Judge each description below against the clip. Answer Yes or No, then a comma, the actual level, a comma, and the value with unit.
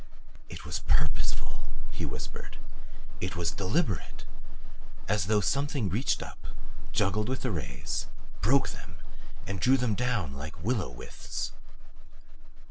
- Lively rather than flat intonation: Yes, wide, 6.4 semitones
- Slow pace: Yes, slow, 125 wpm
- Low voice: Yes, low, 100 Hz